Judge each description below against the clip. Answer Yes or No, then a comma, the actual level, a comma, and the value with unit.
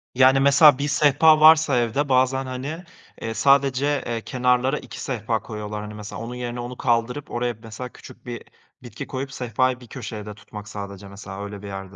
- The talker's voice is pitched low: Yes, low, 125 Hz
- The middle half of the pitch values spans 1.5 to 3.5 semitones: No, average, 4.0 semitones